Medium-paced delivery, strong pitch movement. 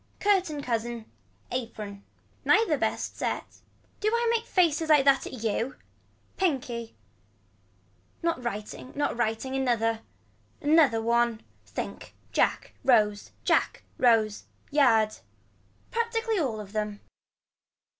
No: slow, 105 wpm; wide, 5.9 semitones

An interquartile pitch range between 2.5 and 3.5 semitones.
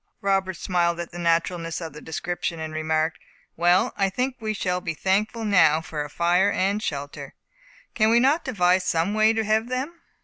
No: average, 4.5 semitones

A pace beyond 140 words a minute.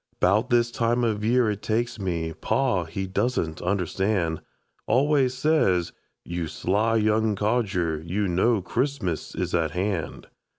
No: slow, 135 wpm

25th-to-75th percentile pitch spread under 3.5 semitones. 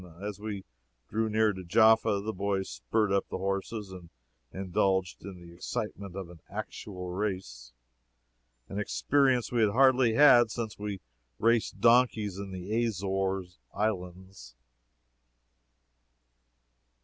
Yes: average, 2.8 semitones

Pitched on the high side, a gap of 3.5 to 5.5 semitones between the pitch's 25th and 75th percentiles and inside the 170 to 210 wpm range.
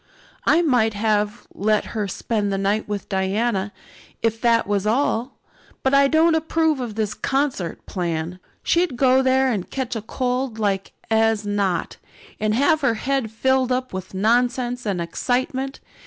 No: high, 230 Hz; average, 4.3 semitones; average, 155 wpm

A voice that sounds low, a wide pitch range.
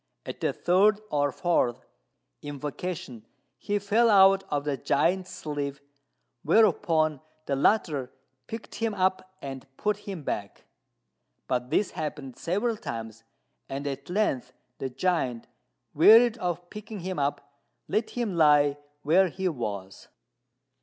No: medium, 165 Hz; wide, 5.9 semitones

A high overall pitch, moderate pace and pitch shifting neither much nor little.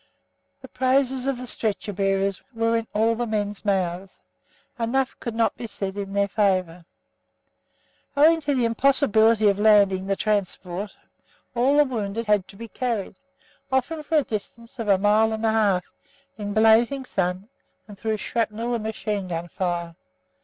Yes: high, 215 Hz; average, 165 wpm; average, 3.1 semitones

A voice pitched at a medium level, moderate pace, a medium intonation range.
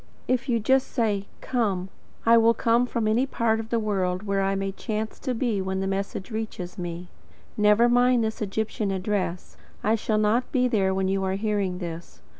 No: high, 210 Hz; average, 195 wpm; average, 3.1 semitones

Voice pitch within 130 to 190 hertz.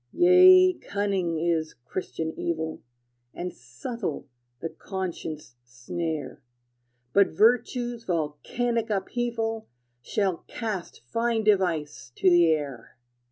Yes: medium, 185 Hz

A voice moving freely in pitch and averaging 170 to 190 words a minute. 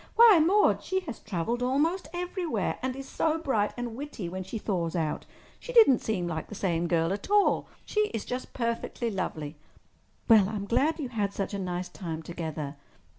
Yes: wide, 8.6 semitones; average, 180 wpm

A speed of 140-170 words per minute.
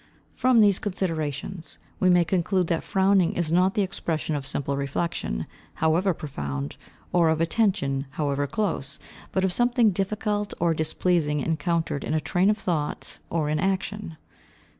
Yes: average, 150 wpm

